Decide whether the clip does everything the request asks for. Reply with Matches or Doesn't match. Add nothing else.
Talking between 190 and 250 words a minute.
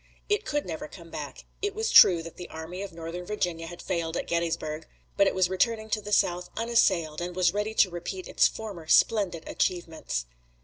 Matches